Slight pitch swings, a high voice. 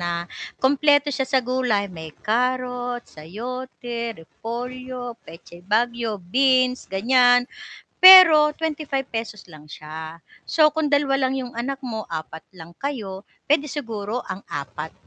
No: wide, 5.4 semitones; high, 245 Hz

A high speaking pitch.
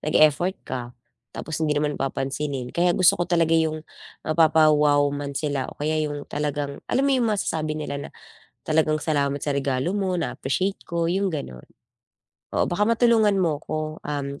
No: medium, 155 Hz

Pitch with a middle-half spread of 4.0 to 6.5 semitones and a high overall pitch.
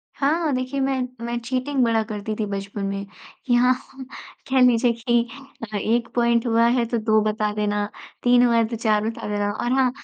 No: average, 2.7 semitones; high, 230 Hz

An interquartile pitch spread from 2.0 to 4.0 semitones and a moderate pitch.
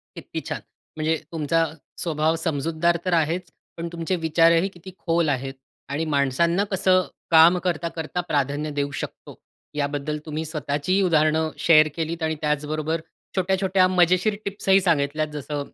Yes: narrow, 2.6 semitones; medium, 160 Hz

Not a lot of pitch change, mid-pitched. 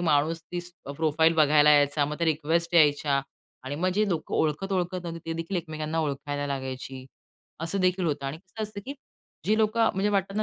No: average, 3.9 semitones; medium, 160 Hz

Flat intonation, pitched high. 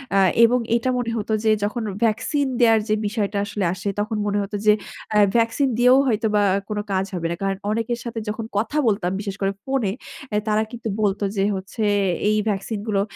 Yes: narrow, 2.2 semitones; high, 215 Hz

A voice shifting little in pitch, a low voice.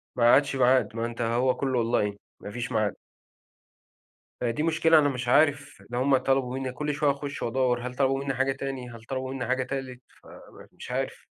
Yes: narrow, 2.1 semitones; low, 130 Hz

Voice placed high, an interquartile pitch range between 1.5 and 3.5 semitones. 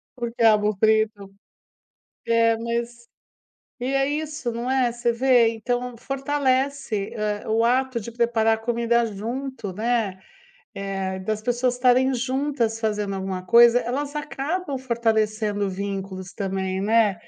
Yes: high, 235 Hz; average, 3.2 semitones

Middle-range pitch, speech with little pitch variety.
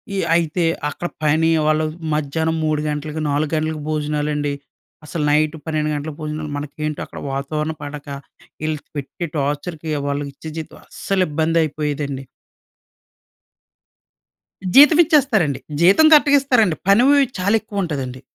Yes: medium, 155 Hz; narrow, 2.3 semitones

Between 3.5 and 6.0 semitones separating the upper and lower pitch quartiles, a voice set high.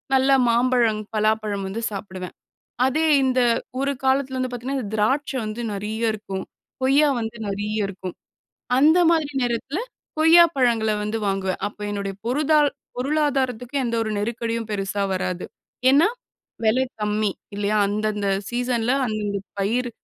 Yes: average, 4.0 semitones; high, 230 Hz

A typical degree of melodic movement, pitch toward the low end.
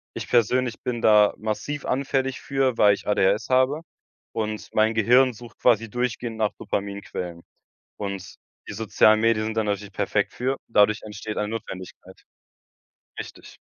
Yes: average, 3.1 semitones; low, 110 Hz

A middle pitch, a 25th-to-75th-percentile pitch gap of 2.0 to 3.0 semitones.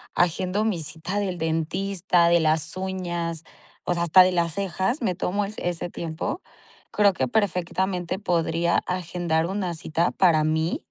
Yes: medium, 175 Hz; narrow, 2.5 semitones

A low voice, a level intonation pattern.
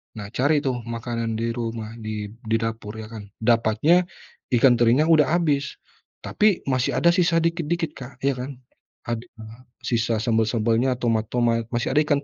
No: low, 120 Hz; average, 3.9 semitones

